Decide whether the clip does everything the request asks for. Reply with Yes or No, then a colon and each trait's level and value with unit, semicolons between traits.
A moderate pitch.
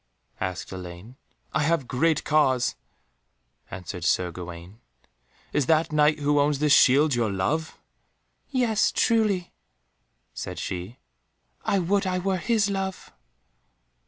Yes: medium, 150 Hz